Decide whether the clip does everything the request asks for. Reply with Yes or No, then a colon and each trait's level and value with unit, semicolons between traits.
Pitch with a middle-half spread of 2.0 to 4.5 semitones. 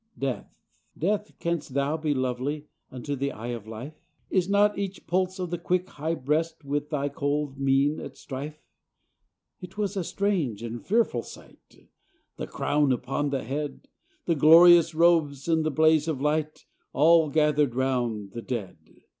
Yes: average, 3.8 semitones